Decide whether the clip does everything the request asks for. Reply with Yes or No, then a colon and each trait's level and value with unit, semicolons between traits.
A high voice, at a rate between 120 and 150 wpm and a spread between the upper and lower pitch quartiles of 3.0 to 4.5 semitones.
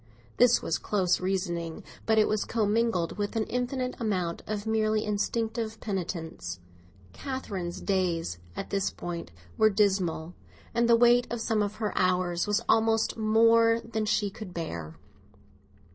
Yes: high, 210 Hz; average, 145 wpm; average, 3.7 semitones